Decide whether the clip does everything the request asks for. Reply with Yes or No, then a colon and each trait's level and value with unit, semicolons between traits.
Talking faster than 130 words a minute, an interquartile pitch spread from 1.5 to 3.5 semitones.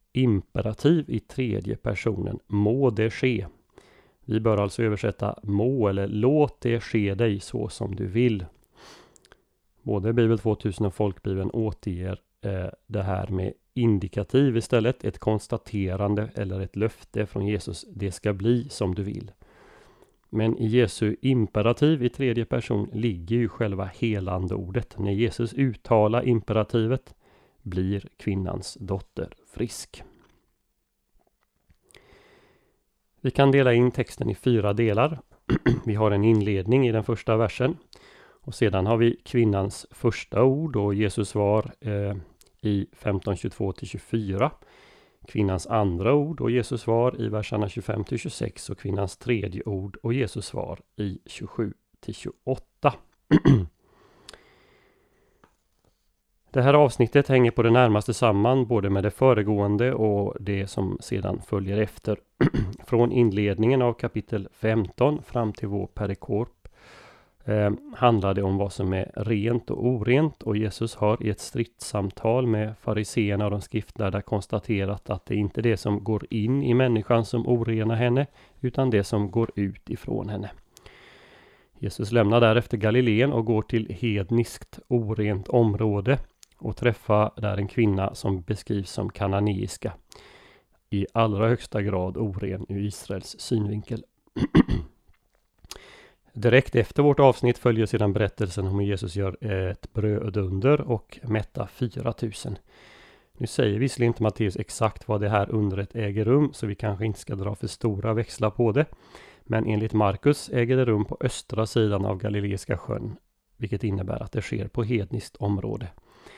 Yes: average, 140 wpm; average, 2.9 semitones